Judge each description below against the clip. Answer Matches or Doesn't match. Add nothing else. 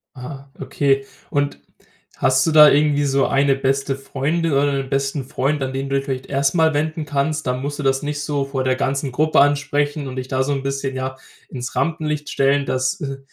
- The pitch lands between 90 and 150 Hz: Matches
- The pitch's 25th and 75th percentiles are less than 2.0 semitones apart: Matches